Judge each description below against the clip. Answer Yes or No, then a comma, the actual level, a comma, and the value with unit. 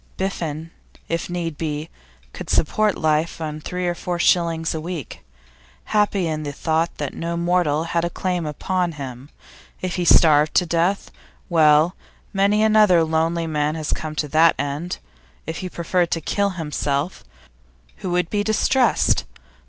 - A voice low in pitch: No, medium, 165 Hz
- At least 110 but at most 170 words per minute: Yes, average, 155 wpm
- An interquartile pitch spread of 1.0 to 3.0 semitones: Yes, average, 2.7 semitones